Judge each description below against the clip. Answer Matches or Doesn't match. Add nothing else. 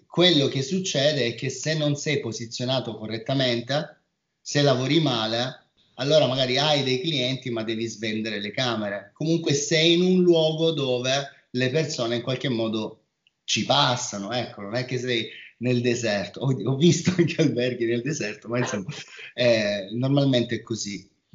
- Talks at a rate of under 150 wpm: Doesn't match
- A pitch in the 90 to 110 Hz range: Doesn't match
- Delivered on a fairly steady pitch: Doesn't match